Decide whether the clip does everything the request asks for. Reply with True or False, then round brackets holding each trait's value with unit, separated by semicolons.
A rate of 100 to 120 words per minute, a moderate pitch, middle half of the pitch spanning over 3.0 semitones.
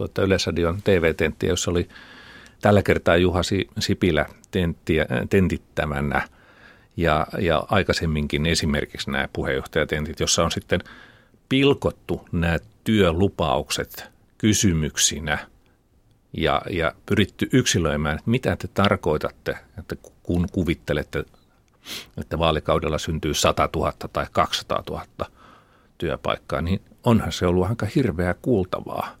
False (105 wpm; 90 Hz; 4.0 semitones)